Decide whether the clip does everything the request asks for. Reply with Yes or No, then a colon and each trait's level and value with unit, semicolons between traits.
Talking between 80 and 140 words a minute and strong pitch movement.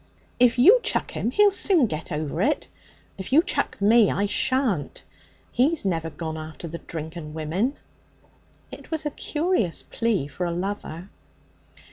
No: average, 155 wpm; wide, 8.7 semitones